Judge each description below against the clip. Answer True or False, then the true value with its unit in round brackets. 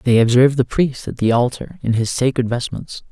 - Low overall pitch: True (125 Hz)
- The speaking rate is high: True (210 wpm)